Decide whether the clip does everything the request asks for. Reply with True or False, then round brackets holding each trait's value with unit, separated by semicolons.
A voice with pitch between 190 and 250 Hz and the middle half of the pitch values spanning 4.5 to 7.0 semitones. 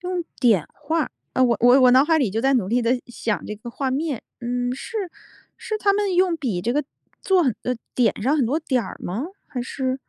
False (260 Hz; 4.8 semitones)